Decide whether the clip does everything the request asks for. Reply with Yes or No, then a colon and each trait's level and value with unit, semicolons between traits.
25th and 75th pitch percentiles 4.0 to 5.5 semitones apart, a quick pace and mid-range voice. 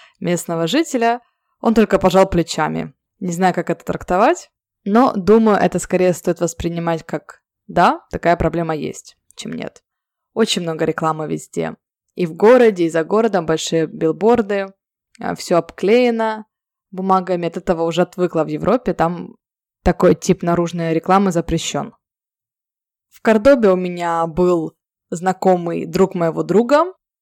No: average, 4.4 semitones; average, 130 wpm; medium, 180 Hz